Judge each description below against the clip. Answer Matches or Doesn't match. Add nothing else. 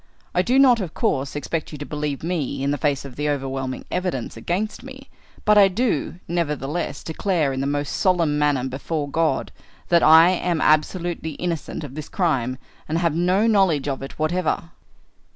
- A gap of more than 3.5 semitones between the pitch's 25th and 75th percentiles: Matches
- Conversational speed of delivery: Matches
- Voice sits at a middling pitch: Matches